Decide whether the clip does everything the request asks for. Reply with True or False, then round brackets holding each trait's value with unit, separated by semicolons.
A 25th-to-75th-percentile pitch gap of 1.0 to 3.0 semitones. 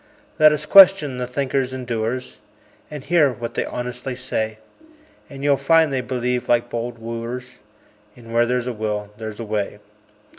True (2.7 semitones)